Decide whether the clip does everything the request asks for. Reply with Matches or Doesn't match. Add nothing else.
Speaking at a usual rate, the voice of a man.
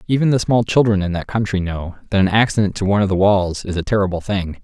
Doesn't match